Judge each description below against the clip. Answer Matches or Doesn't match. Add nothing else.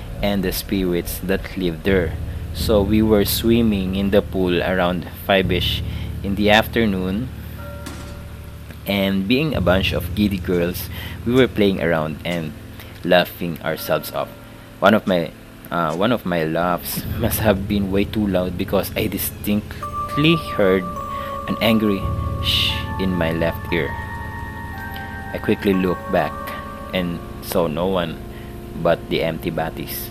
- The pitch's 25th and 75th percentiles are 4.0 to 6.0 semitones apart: Doesn't match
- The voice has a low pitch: Matches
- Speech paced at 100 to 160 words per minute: Matches